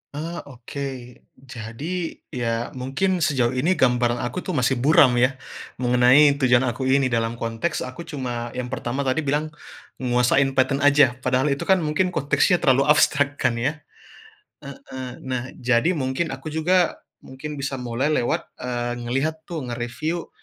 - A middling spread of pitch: Yes, average, 3.4 semitones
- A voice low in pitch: Yes, low, 130 Hz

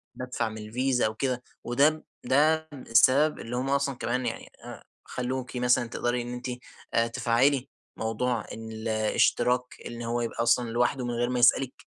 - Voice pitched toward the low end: Yes, low, 125 Hz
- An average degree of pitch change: No, narrow, 1.8 semitones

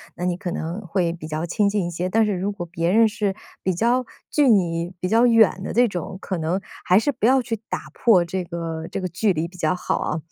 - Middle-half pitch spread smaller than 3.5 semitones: No, average, 3.8 semitones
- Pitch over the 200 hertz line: No, medium, 185 Hz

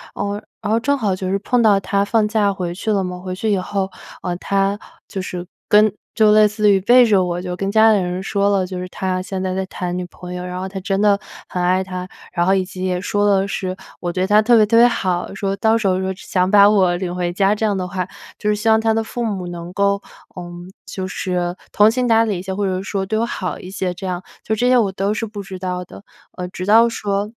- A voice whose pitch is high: Yes, high, 195 Hz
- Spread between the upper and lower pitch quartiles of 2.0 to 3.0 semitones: Yes, narrow, 2.4 semitones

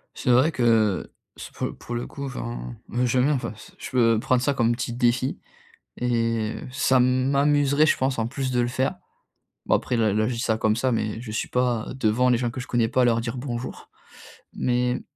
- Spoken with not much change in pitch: Yes, narrow, 2.0 semitones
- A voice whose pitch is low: Yes, low, 125 Hz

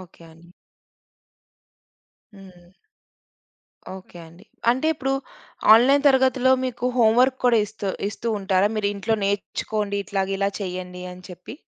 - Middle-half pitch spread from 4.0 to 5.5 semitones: Yes, average, 4.9 semitones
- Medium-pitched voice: No, high, 205 Hz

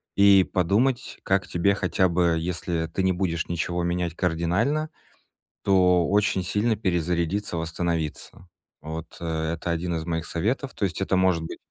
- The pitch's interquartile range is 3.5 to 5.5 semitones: No, average, 2.7 semitones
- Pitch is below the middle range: Yes, very low, 90 Hz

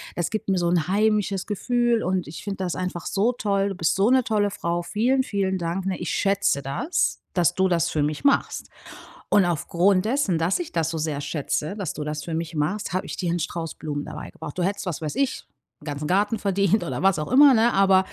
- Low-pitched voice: No, medium, 185 Hz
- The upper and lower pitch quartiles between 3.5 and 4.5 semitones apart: Yes, average, 3.8 semitones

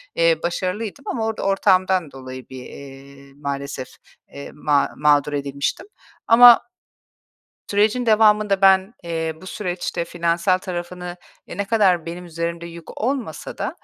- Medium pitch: Yes, medium, 175 Hz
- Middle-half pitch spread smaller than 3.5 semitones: No, average, 5.2 semitones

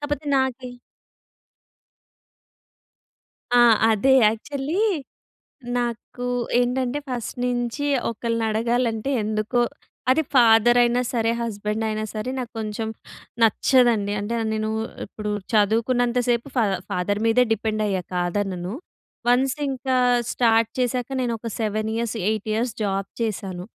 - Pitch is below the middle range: No, high, 230 Hz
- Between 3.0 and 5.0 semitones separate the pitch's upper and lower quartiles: No, narrow, 2.5 semitones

